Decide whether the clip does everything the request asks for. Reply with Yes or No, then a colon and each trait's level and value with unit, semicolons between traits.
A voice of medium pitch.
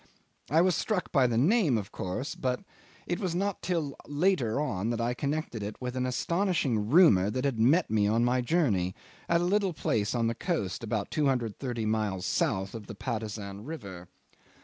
No: low, 125 Hz